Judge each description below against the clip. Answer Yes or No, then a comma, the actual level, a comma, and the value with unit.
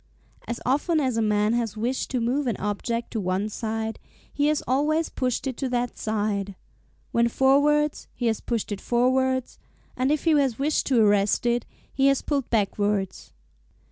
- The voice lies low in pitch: No, high, 240 Hz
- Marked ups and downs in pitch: No, average, 3.9 semitones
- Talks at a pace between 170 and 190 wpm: Yes, average, 175 wpm